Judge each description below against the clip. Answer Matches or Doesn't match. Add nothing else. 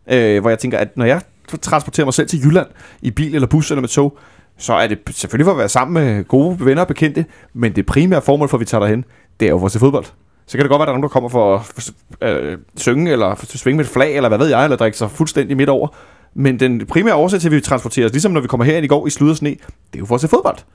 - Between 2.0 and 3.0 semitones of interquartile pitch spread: Doesn't match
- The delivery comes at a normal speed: Doesn't match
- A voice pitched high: Doesn't match